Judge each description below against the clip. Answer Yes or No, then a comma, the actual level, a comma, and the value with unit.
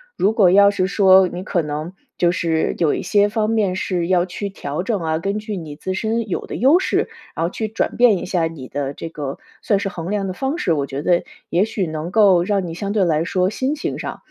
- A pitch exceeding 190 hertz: No, medium, 185 Hz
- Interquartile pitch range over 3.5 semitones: Yes, average, 3.9 semitones